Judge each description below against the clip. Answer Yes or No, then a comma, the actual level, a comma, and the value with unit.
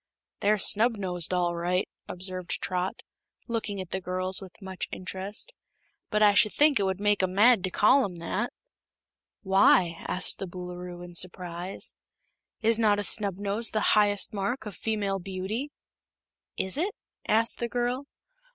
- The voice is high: Yes, high, 195 Hz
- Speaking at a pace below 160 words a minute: Yes, average, 150 wpm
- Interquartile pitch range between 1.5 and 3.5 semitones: Yes, average, 2.8 semitones